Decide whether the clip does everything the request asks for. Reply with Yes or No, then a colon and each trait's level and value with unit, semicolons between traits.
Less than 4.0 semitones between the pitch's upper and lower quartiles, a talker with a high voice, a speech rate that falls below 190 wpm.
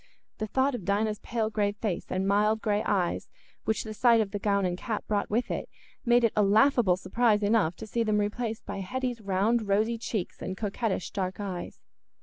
No: narrow, 2.4 semitones; high, 210 Hz; average, 200 wpm